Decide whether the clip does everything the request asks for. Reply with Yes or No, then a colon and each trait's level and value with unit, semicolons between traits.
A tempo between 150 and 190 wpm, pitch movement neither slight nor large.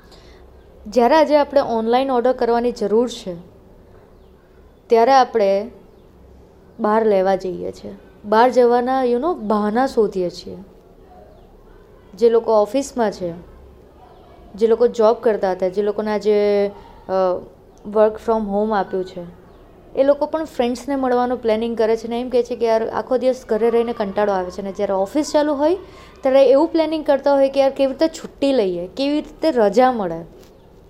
Yes: fast, 155 wpm; average, 4.3 semitones